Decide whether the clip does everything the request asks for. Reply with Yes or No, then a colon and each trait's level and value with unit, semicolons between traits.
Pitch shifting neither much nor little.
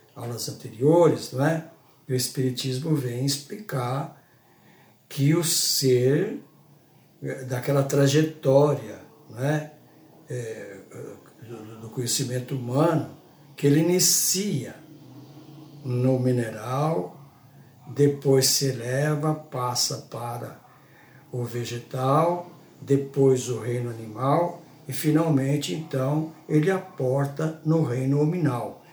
Yes: average, 3.2 semitones